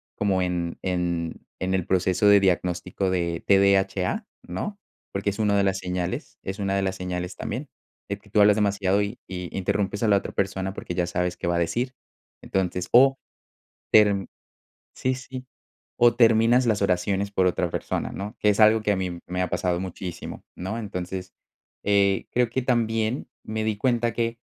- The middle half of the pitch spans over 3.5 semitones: No, average, 2.9 semitones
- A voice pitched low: Yes, low, 100 Hz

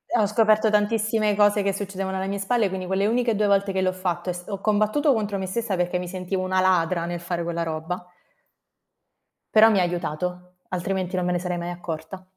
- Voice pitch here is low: No, high, 190 Hz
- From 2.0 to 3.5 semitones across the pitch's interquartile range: Yes, narrow, 2.5 semitones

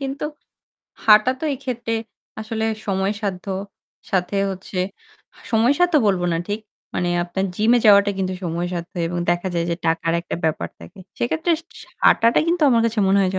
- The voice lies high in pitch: Yes, high, 200 Hz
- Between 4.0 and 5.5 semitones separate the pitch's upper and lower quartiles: Yes, average, 4.6 semitones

